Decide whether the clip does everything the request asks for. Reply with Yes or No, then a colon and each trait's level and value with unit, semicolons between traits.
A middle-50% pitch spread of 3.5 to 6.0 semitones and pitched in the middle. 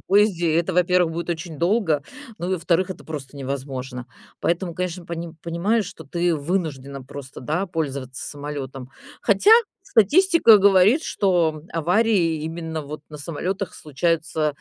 Yes: average, 3.9 semitones; medium, 165 Hz